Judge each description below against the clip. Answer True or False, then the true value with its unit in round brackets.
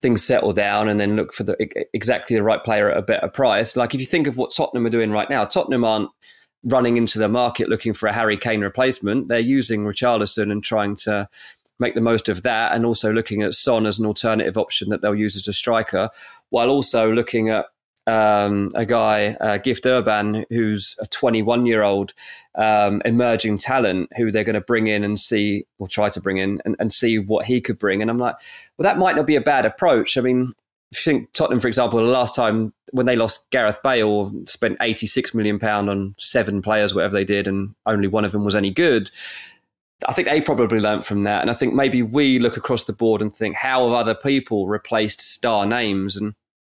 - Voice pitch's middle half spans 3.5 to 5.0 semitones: False (2.6 semitones)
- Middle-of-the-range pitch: False (110 Hz)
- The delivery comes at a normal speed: False (225 wpm)